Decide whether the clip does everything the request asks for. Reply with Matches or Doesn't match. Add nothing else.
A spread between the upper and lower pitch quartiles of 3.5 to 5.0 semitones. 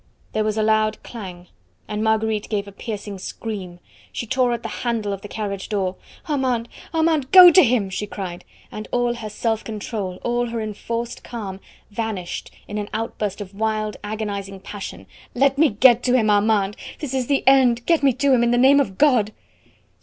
Doesn't match